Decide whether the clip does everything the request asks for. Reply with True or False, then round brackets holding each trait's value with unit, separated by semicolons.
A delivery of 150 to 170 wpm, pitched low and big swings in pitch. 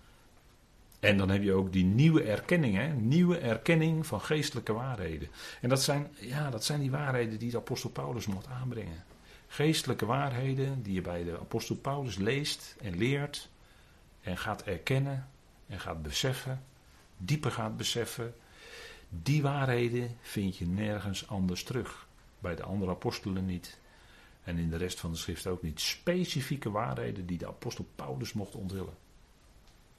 True (155 wpm; 115 Hz; 6.3 semitones)